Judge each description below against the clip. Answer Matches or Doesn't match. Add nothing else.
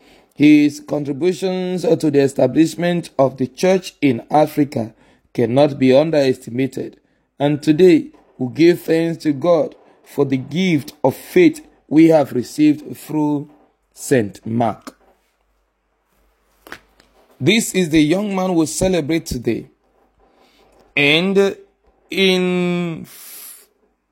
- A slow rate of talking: Matches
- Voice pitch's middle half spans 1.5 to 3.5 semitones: Doesn't match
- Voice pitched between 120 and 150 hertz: Doesn't match